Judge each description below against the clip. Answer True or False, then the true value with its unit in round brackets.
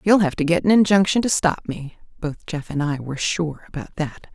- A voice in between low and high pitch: True (165 Hz)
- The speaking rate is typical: False (235 wpm)